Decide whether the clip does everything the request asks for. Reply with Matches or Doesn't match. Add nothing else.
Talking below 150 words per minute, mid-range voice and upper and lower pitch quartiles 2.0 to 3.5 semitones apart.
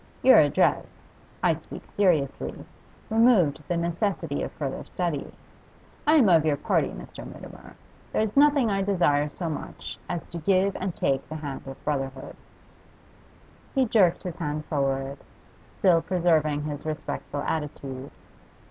Doesn't match